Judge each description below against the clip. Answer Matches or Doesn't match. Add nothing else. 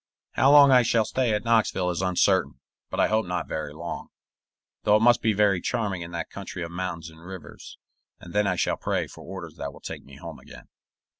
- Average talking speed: Doesn't match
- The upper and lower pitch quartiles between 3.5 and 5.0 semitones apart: Matches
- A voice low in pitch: Matches